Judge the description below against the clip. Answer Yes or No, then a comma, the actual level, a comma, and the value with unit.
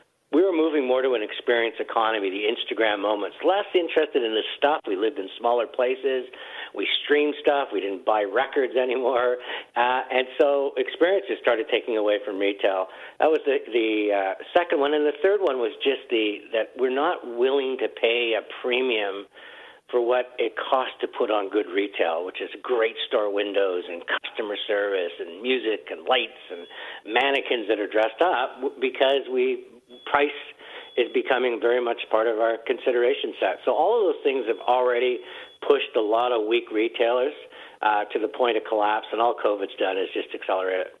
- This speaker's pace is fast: No, average, 185 wpm